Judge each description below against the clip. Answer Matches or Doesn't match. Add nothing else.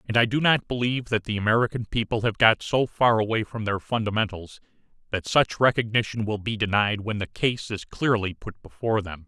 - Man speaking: Matches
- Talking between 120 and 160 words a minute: Doesn't match